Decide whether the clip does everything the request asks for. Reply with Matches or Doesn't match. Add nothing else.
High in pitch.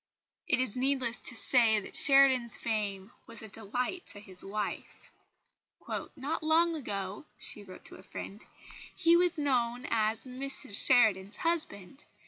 Matches